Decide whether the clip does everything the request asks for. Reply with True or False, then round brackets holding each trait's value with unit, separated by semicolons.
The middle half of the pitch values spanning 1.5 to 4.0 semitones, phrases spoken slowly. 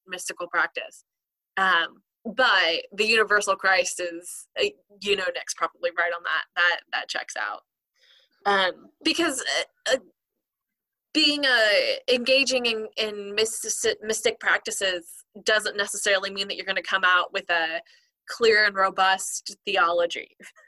False (4.7 semitones; 130 wpm)